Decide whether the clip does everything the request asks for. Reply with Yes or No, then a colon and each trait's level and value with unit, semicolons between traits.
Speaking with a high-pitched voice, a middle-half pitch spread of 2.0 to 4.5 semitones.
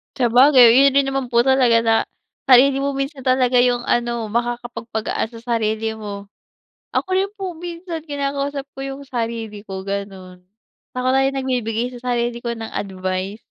Yes: high, 240 Hz; average, 3.4 semitones